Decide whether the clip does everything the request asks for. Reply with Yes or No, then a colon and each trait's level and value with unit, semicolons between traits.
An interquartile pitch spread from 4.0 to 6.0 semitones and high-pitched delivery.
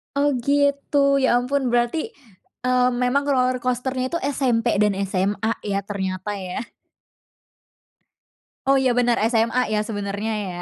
Yes: average, 4.5 semitones; high, 245 Hz